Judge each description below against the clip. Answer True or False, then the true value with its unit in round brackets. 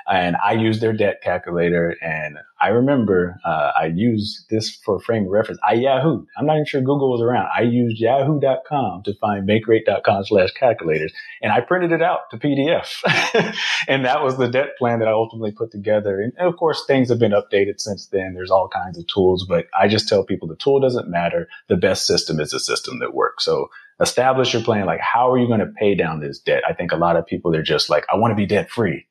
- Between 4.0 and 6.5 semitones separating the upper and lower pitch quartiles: True (5.2 semitones)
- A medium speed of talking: False (230 wpm)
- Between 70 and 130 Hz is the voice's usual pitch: True (115 Hz)